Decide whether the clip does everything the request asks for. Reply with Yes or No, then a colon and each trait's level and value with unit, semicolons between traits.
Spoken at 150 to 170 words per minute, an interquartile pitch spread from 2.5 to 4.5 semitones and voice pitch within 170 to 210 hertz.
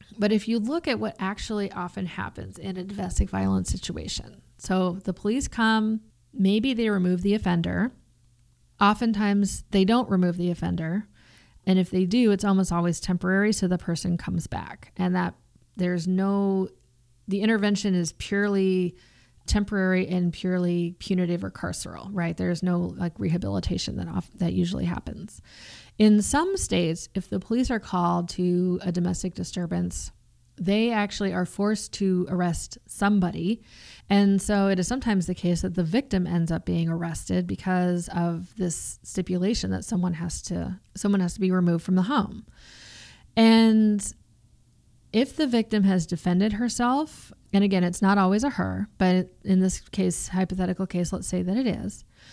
Yes: average, 160 wpm; average, 2.9 semitones; medium, 185 Hz